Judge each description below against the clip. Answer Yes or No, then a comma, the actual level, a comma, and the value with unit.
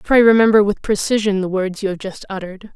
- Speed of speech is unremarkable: No, fast, 220 wpm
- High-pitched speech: Yes, high, 200 Hz